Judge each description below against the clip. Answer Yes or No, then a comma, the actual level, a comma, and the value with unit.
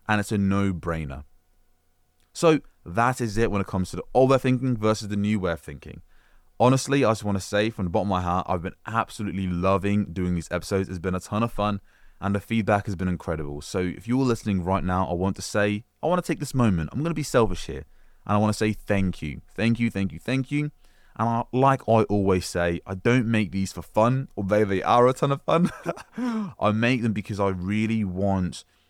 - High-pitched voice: No, low, 100 Hz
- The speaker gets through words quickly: Yes, fast, 240 wpm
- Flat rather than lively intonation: No, average, 4.2 semitones